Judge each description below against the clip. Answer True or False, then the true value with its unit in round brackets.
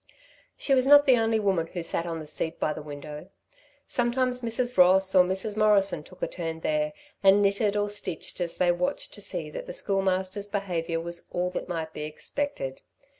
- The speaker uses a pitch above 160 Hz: True (190 Hz)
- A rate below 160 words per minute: False (195 wpm)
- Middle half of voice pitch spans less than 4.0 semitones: False (5.0 semitones)